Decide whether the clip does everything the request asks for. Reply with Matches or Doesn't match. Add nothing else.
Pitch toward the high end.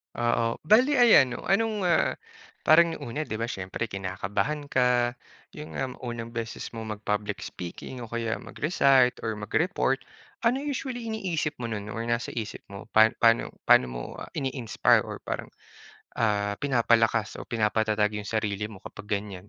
Doesn't match